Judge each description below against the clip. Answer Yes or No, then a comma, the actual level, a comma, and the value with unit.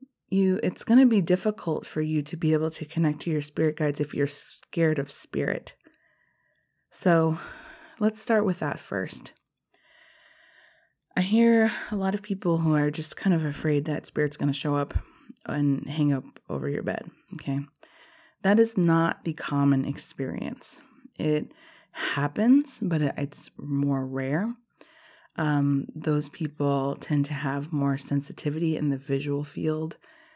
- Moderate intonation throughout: No, wide, 7.1 semitones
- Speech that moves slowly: No, average, 150 wpm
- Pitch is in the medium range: Yes, medium, 160 Hz